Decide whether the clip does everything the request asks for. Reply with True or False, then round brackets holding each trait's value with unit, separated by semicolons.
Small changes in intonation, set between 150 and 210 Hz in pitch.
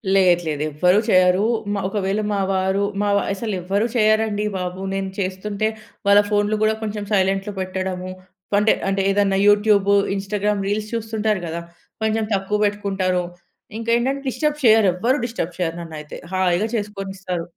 True (2.2 semitones; 200 Hz)